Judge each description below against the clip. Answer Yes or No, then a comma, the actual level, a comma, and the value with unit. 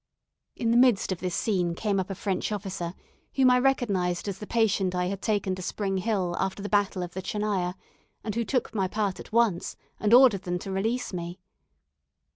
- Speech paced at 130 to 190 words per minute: No, fast, 205 wpm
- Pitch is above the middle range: Yes, high, 195 Hz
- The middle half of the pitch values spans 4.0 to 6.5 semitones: No, average, 3.1 semitones